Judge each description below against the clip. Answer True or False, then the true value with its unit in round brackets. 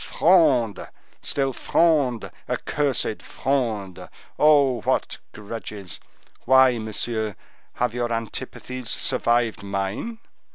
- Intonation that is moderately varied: True (3.7 semitones)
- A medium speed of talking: False (85 wpm)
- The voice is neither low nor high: False (120 Hz)